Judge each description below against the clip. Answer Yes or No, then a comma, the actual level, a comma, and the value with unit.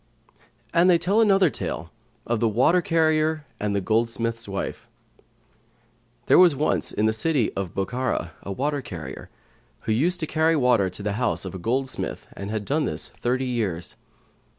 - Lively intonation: Yes, wide, 7.2 semitones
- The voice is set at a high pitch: No, low, 120 Hz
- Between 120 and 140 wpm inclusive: No, average, 170 wpm